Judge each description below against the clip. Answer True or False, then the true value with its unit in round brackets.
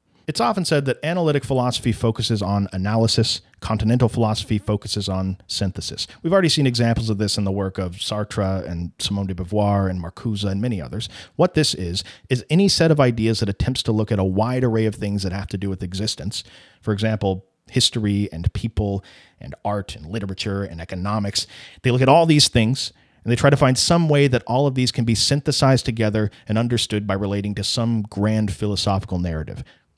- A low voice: True (110 Hz)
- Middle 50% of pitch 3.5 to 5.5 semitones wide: True (3.8 semitones)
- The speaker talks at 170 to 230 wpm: True (200 wpm)